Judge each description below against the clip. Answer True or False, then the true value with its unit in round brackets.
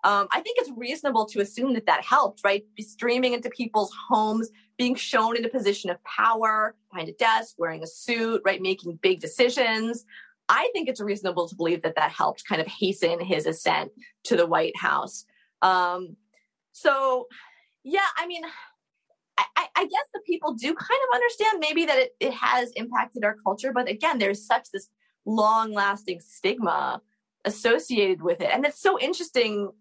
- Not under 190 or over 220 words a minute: False (175 wpm)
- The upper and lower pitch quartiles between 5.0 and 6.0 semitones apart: True (5.4 semitones)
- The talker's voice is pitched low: False (225 Hz)